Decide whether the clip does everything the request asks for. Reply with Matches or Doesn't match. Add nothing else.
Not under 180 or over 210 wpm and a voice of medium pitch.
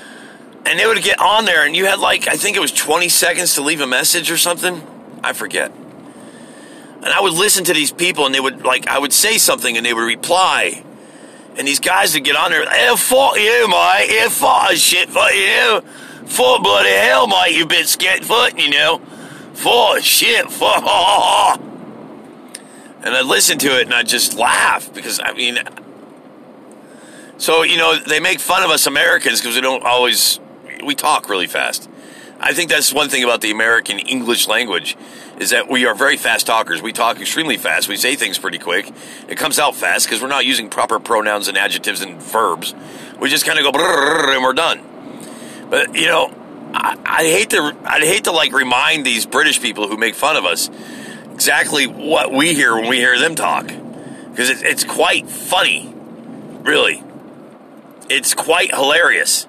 Matches